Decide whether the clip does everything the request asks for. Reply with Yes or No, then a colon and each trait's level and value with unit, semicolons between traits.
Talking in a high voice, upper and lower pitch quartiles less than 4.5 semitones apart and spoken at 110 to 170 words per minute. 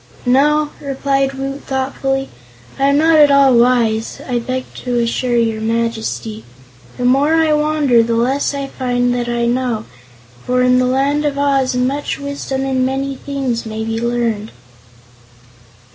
Yes: very high, 260 Hz; average, 2.7 semitones; average, 155 wpm